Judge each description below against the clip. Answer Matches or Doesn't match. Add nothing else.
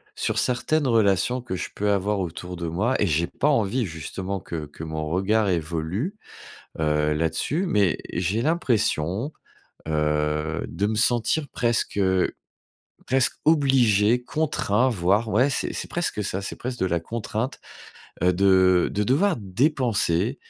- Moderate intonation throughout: Doesn't match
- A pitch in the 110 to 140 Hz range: Doesn't match